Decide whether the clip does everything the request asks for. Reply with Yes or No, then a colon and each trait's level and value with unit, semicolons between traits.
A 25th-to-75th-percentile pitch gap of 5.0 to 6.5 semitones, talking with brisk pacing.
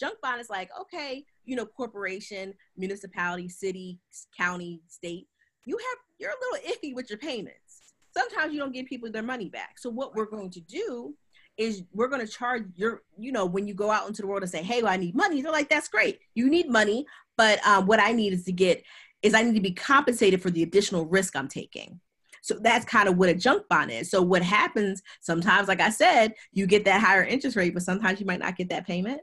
Yes: wide, 5.4 semitones; fast, 235 wpm